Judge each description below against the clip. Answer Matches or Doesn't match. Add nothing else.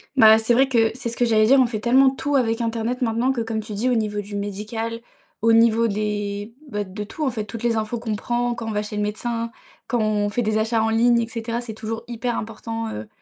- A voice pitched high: Matches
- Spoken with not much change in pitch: Matches